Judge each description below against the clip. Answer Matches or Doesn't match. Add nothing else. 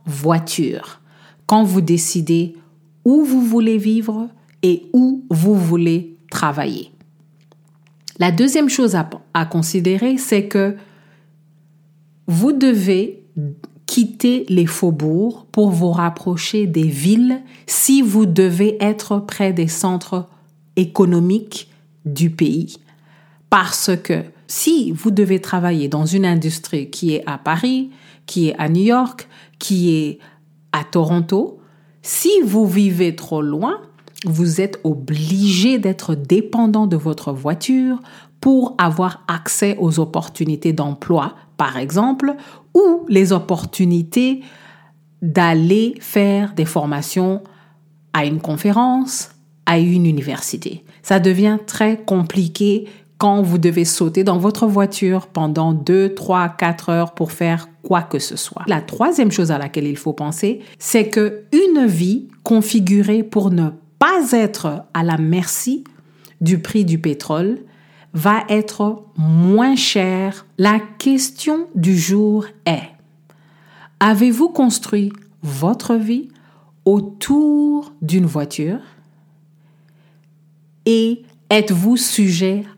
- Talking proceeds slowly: Matches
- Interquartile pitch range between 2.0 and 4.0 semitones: Doesn't match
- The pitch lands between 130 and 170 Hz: Doesn't match